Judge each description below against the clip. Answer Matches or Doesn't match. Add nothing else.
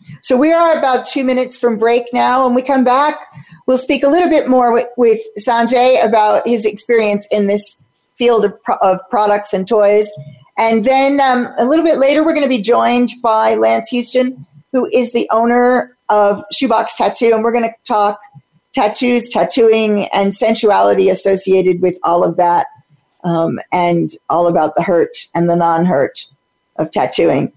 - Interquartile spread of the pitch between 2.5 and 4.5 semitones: Doesn't match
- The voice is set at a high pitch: Matches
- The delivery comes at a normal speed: Matches